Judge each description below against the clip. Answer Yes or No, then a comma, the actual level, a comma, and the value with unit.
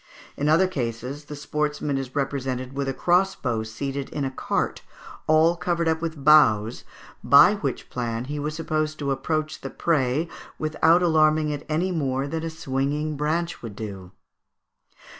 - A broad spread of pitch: No, average, 2.9 semitones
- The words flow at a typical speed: Yes, average, 160 wpm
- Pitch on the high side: No, medium, 150 Hz